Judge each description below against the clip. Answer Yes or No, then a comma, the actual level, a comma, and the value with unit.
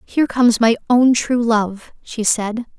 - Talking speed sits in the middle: Yes, average, 170 wpm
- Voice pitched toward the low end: No, high, 230 Hz